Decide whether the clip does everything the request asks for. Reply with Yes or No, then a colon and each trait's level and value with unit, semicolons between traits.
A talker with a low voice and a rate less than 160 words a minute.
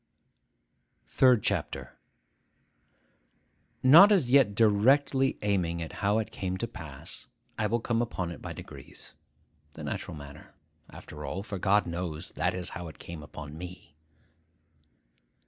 Yes: low, 100 Hz; slow, 135 wpm